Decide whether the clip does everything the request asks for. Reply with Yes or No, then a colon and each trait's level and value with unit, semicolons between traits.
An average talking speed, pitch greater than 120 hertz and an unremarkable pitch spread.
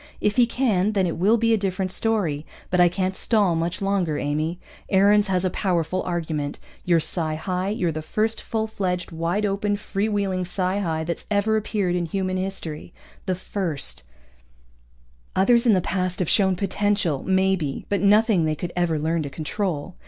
Yes: average, 180 wpm; medium, 185 Hz; average, 3.3 semitones